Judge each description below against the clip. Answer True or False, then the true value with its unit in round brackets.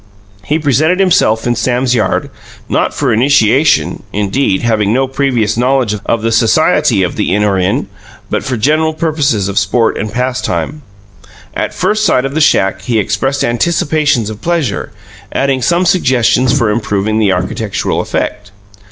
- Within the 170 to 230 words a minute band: False (155 wpm)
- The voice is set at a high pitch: False (125 Hz)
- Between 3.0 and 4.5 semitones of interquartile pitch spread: False (5.1 semitones)